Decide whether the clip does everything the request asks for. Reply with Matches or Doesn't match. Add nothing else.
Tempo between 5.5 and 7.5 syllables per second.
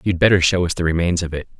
Matches